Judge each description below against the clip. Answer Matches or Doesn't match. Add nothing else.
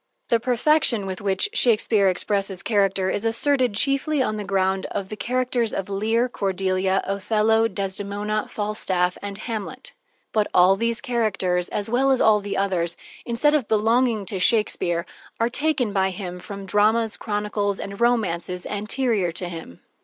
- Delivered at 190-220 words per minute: Doesn't match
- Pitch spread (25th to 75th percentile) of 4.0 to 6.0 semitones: Doesn't match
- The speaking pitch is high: Matches